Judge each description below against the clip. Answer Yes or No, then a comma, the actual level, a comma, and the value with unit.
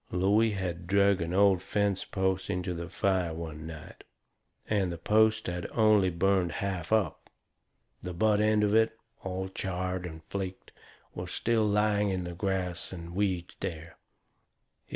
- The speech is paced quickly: No, average, 150 wpm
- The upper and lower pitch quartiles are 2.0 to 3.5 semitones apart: Yes, narrow, 2.6 semitones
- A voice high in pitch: No, very low, 95 Hz